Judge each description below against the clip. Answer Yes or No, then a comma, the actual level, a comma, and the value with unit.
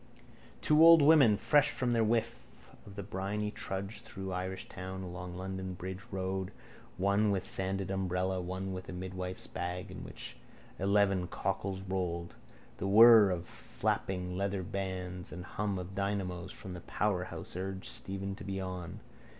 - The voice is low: Yes, very low, 95 Hz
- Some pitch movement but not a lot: No, narrow, 1.5 semitones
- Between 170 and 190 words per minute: No, average, 160 wpm